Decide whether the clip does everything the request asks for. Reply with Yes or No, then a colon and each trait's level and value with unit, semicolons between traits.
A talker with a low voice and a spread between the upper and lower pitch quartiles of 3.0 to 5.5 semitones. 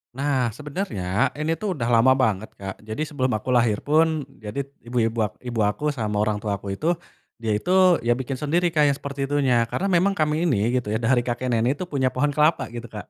Yes: low, 130 Hz; average, 4.8 semitones